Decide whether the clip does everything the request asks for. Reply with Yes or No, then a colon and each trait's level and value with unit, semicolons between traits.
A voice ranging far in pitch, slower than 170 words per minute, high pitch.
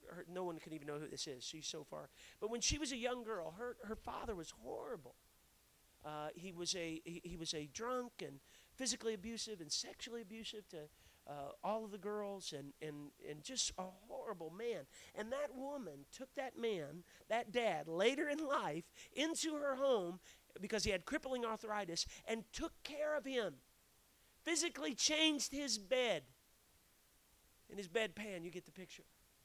No: wide, 7.0 semitones; average, 175 wpm; high, 215 Hz